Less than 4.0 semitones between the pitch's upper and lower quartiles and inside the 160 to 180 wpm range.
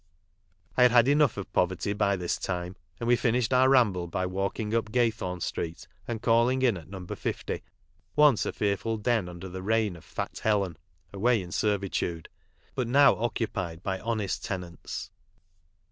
No: average, 4.3 semitones; average, 170 wpm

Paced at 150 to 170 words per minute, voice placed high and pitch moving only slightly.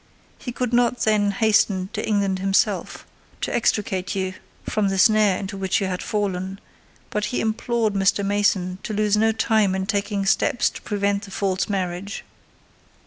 Yes: average, 165 wpm; high, 200 Hz; narrow, 2.0 semitones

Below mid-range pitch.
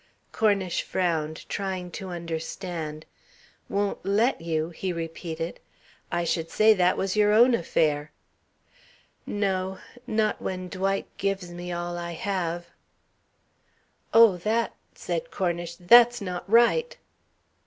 No: medium, 185 Hz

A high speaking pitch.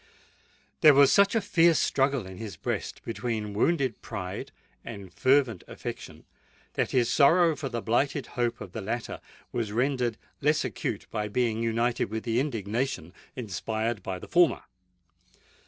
No: low, 120 Hz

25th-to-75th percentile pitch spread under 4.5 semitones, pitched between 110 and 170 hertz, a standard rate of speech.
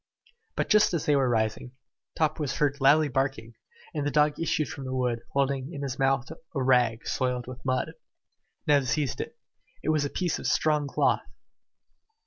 Yes: average, 2.7 semitones; low, 135 Hz; average, 180 wpm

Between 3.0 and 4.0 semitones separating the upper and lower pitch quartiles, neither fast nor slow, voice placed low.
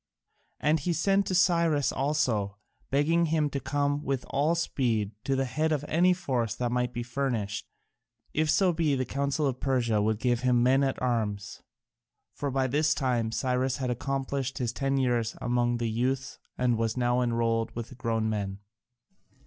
Yes: average, 3.3 semitones; average, 175 wpm; low, 130 Hz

